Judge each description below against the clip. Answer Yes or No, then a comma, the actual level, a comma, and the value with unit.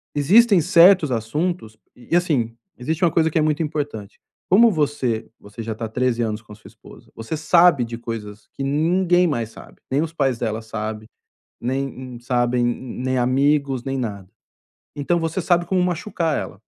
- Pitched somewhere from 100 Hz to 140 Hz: Yes, low, 135 Hz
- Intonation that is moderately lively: No, wide, 6.1 semitones